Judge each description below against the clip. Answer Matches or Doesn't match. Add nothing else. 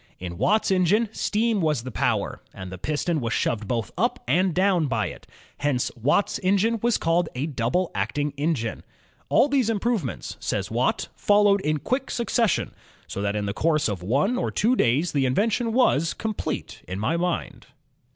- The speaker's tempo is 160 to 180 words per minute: Matches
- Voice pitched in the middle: Matches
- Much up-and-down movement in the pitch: Matches